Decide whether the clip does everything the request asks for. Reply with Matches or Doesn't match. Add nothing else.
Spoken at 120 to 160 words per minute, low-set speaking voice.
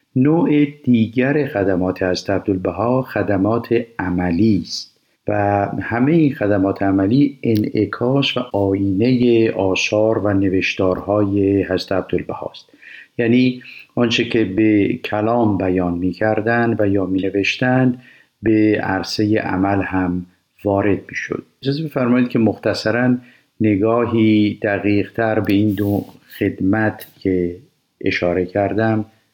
Doesn't match